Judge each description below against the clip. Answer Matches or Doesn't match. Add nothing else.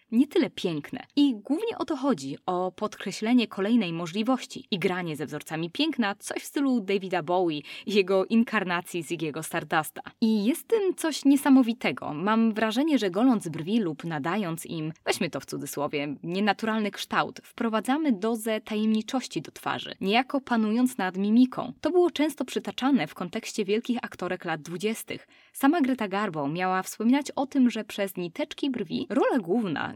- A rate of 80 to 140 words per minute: Doesn't match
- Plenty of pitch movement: Matches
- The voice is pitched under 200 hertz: Doesn't match